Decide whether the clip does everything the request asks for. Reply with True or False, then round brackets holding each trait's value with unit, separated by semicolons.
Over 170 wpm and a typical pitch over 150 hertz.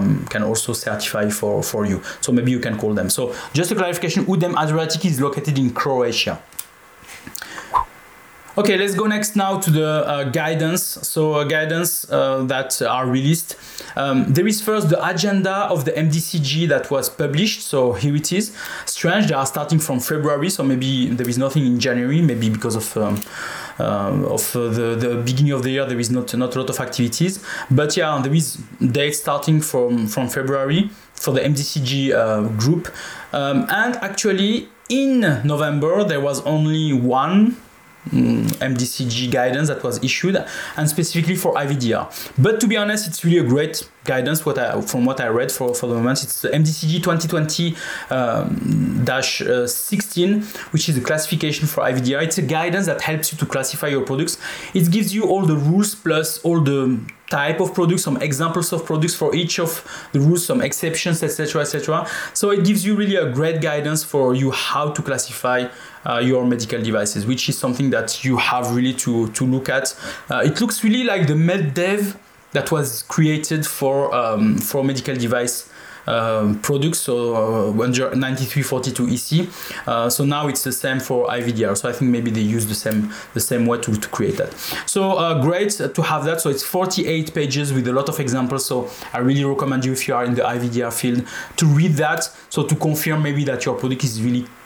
False (190 wpm; 145 Hz)